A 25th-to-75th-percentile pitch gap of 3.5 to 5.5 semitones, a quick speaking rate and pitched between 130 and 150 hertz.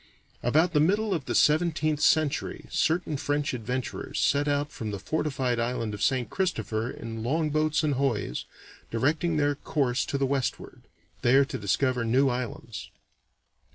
No: average, 4.1 semitones; average, 150 wpm; medium, 140 Hz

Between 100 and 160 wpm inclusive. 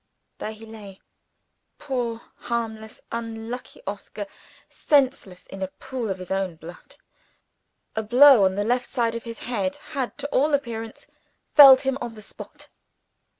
Yes: average, 150 wpm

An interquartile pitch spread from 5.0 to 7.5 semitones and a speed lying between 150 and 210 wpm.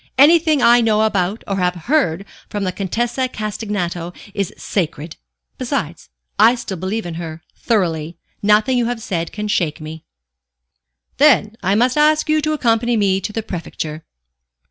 Yes: wide, 5.4 semitones; average, 155 wpm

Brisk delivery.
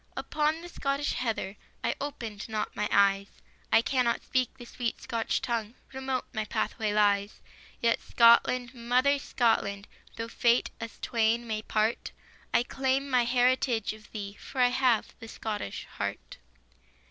No: average, 145 wpm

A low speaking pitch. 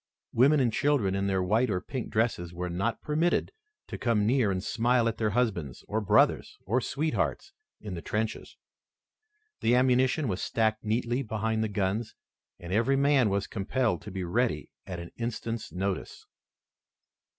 Yes: low, 110 Hz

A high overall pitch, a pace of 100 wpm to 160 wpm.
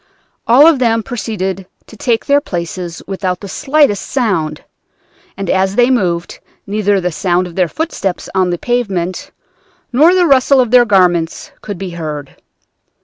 Yes: high, 195 Hz; average, 155 wpm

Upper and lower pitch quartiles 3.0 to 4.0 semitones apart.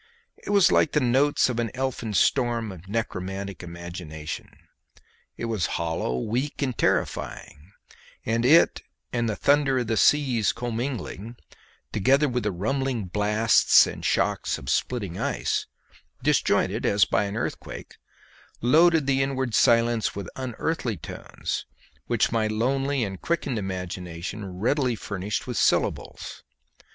No: average, 5.2 semitones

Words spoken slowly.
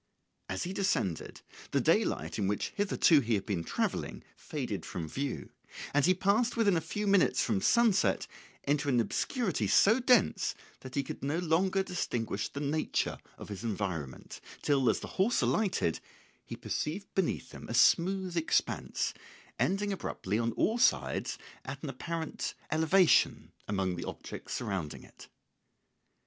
No: average, 155 wpm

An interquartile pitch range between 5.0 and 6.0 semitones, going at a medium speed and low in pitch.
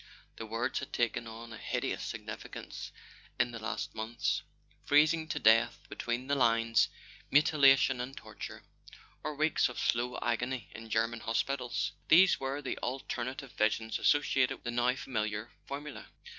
No: average, 3.2 semitones; average, 145 wpm; low, 120 Hz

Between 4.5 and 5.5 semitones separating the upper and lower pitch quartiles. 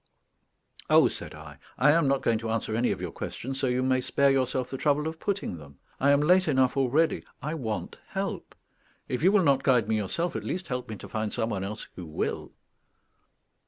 Yes: average, 4.9 semitones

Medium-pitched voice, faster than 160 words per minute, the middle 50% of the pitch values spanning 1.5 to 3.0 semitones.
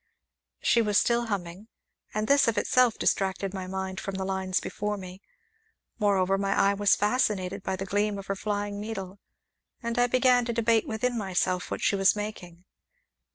No: high, 200 Hz; average, 175 wpm; narrow, 2.6 semitones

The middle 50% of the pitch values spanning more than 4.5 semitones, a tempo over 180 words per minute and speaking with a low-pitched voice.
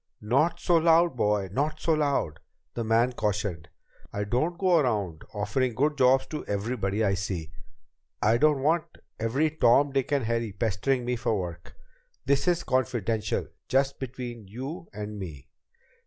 No: wide, 5.4 semitones; average, 155 wpm; low, 120 Hz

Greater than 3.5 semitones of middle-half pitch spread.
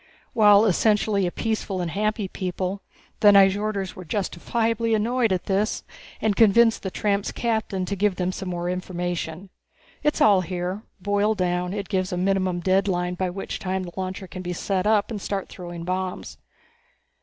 No: narrow, 2.4 semitones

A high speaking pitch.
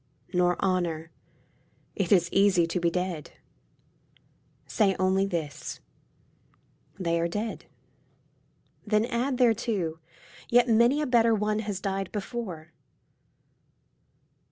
Yes: high, 195 Hz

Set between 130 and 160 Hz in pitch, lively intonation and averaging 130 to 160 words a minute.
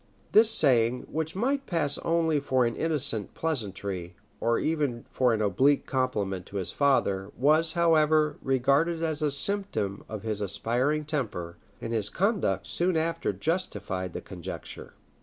Yes: medium, 140 Hz; wide, 7.4 semitones; average, 145 wpm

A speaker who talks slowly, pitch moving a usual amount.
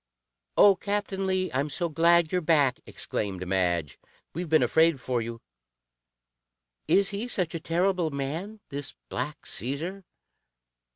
No: slow, 130 wpm; wide, 5.8 semitones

